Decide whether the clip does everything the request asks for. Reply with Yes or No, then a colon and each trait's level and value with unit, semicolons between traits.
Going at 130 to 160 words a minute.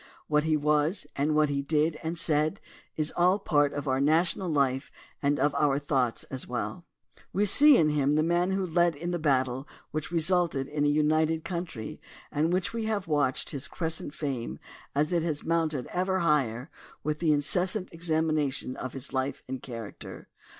No: average, 180 wpm